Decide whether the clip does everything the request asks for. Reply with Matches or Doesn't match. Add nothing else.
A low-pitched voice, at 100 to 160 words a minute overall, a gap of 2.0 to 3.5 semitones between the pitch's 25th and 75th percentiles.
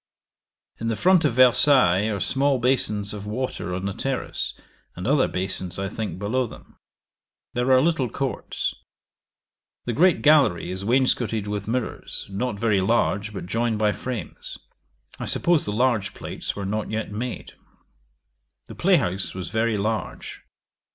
Doesn't match